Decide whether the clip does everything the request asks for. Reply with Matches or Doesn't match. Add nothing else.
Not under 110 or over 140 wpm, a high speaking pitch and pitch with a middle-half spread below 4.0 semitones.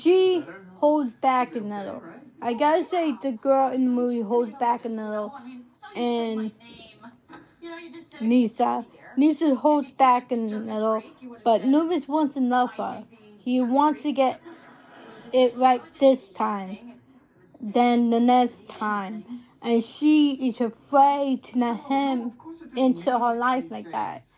Matches